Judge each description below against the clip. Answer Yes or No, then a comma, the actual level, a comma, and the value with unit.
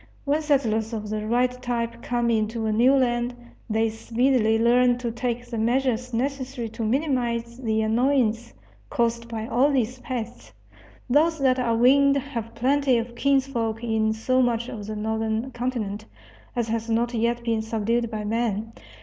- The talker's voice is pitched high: Yes, high, 235 Hz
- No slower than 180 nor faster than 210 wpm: No, average, 160 wpm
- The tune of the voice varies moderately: No, narrow, 2.2 semitones